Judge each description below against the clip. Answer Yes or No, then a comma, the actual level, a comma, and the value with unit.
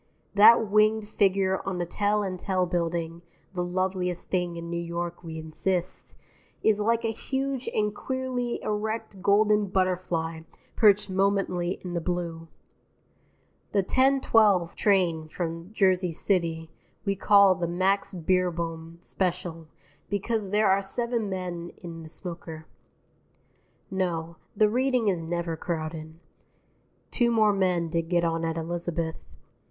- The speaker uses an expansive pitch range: No, average, 3.5 semitones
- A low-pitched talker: No, medium, 185 Hz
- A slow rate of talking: Yes, slow, 130 wpm